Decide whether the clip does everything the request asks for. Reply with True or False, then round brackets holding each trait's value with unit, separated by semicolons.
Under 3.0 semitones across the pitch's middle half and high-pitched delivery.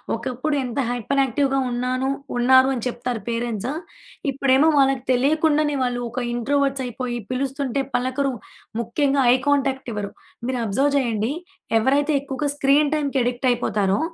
True (2.4 semitones; 260 Hz)